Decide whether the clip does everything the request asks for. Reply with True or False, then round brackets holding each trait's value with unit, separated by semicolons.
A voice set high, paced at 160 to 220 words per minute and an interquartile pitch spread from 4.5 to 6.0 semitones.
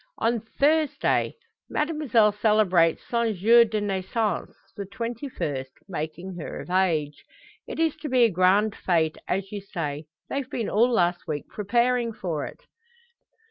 False (205 Hz; 145 wpm; 5.1 semitones)